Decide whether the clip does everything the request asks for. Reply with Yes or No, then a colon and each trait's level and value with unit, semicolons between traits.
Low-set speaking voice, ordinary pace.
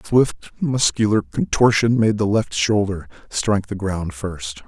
Yes: low, 105 Hz; average, 155 wpm